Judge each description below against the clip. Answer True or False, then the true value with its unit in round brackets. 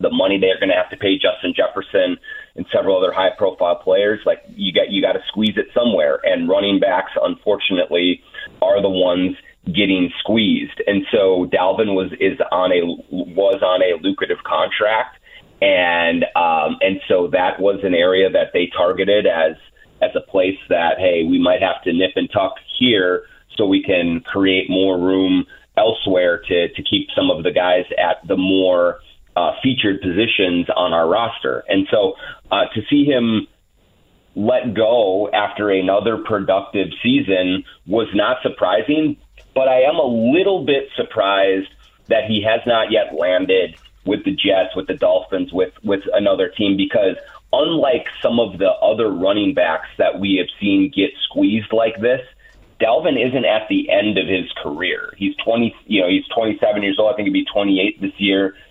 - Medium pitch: False (100 Hz)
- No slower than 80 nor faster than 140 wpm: False (175 wpm)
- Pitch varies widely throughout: True (7.9 semitones)